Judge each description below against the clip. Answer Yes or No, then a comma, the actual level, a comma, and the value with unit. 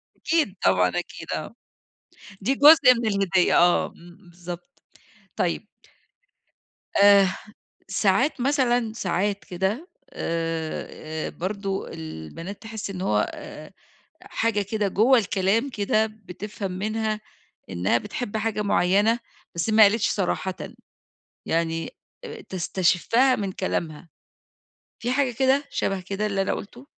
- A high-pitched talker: Yes, high, 200 Hz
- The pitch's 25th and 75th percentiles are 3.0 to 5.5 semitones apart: Yes, average, 4.2 semitones